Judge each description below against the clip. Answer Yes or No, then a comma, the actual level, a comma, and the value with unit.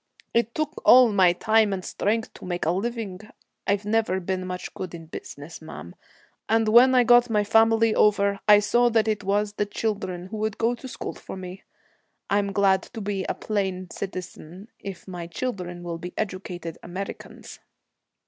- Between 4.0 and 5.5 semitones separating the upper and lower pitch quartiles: No, average, 3.4 semitones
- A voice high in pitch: Yes, high, 200 Hz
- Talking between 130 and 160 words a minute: No, average, 175 wpm